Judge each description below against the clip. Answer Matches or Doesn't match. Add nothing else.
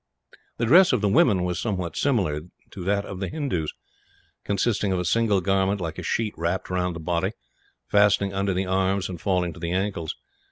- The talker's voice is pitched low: Matches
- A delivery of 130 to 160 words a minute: Doesn't match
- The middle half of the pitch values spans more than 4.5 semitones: Doesn't match